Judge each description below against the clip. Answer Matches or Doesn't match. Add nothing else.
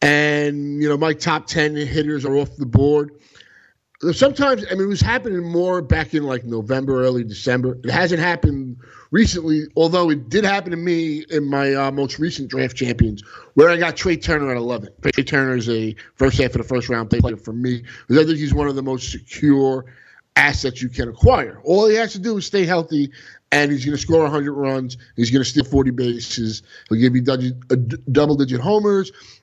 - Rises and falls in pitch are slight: Doesn't match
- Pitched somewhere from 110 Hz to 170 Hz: Matches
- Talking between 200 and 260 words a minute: Matches